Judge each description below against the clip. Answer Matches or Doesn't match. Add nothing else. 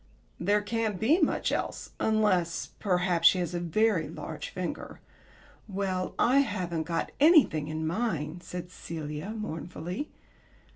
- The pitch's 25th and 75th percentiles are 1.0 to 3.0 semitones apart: Doesn't match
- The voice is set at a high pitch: Doesn't match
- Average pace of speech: Doesn't match